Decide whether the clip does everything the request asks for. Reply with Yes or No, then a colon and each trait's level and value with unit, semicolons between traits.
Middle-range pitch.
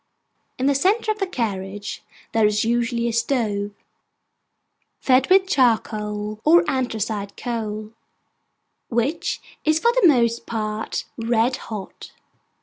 No: high, 235 Hz